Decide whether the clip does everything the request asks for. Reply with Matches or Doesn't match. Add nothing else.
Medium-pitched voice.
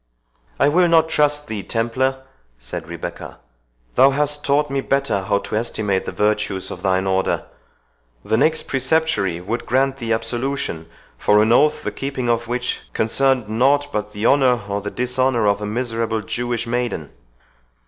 Doesn't match